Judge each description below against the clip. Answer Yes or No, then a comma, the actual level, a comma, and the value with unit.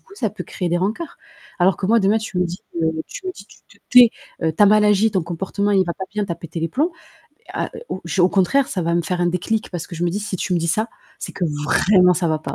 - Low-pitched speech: No, medium, 185 Hz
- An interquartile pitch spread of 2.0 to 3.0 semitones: No, average, 3.6 semitones